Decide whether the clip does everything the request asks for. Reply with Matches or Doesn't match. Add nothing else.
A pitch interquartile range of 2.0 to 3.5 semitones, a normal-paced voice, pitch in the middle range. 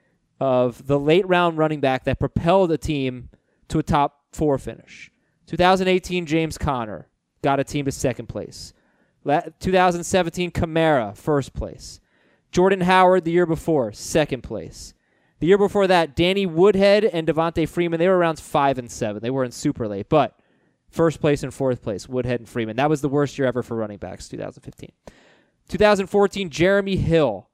Doesn't match